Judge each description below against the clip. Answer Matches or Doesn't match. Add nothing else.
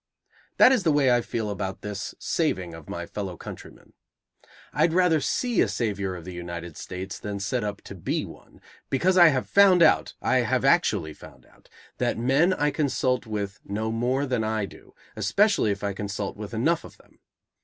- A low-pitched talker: Matches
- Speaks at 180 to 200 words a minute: Matches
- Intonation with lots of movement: Matches